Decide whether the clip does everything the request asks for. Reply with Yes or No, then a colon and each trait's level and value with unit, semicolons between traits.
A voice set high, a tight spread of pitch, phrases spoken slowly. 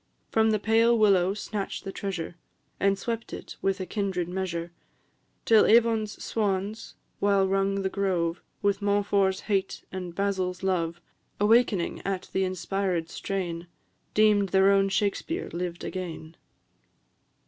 Yes: high, 195 Hz; narrow, 2.0 semitones; slow, 130 wpm